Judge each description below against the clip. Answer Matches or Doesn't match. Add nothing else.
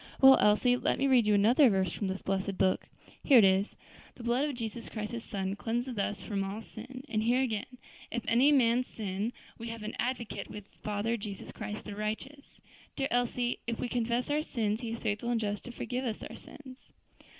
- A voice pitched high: Matches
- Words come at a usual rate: Doesn't match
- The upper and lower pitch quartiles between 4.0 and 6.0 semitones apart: Doesn't match